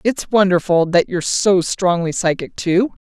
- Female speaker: Yes, female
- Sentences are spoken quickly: No, average, 155 wpm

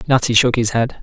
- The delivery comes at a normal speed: No, fast, 235 wpm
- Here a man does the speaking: Yes, male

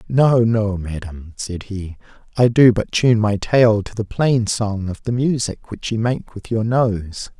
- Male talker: Yes, male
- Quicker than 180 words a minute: Yes, average, 195 wpm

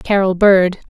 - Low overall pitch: No, high, 190 Hz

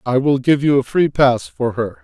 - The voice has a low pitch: Yes, low, 130 Hz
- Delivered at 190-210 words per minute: No, fast, 265 wpm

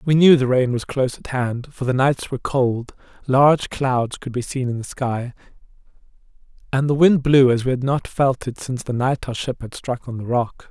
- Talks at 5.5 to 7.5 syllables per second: No, 5.1 syllables/s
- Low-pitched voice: Yes, low, 130 Hz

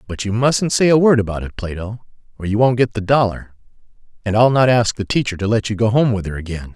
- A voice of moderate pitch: No, low, 110 Hz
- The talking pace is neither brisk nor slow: No, fast, 255 wpm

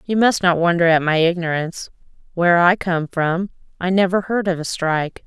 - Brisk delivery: No, average, 195 wpm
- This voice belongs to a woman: Yes, female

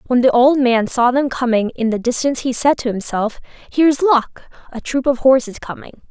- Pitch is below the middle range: No, very high, 250 Hz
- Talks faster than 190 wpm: Yes, fast, 205 wpm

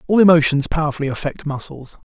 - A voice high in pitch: No, medium, 150 Hz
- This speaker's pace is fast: No, average, 140 wpm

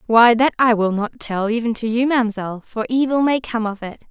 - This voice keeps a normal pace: No, fast, 235 wpm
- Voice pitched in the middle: No, high, 230 Hz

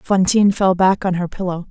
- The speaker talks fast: Yes, fast, 210 wpm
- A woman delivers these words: Yes, female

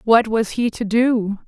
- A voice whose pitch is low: No, high, 225 Hz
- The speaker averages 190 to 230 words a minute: Yes, fast, 205 wpm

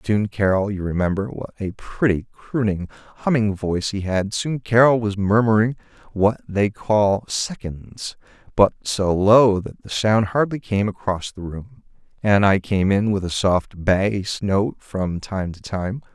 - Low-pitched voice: Yes, low, 105 Hz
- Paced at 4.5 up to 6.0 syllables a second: No, 4.1 syllables/s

